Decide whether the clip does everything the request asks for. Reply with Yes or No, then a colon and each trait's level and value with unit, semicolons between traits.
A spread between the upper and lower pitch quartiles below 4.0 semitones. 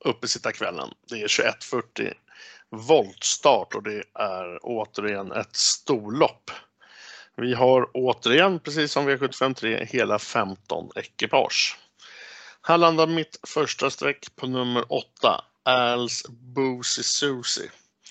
Yes: average, 2.8 semitones